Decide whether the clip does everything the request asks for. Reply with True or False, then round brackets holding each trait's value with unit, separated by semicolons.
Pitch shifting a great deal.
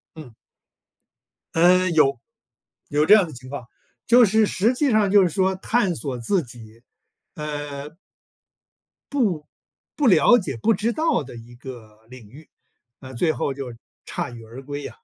True (7.3 semitones)